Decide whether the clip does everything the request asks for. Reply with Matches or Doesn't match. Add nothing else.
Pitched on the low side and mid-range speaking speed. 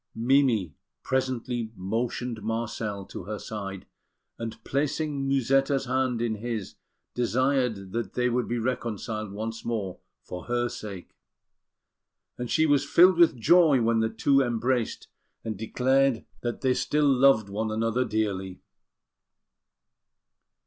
Doesn't match